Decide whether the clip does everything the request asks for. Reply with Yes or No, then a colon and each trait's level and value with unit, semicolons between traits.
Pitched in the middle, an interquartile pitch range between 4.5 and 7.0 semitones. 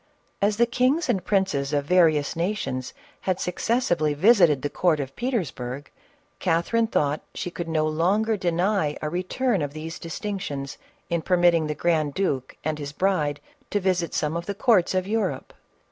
Yes: medium, 175 Hz; average, 4.8 semitones